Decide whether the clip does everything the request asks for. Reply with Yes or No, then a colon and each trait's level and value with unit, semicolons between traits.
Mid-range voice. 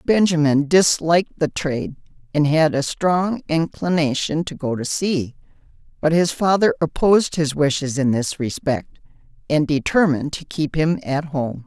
Yes: medium, 155 Hz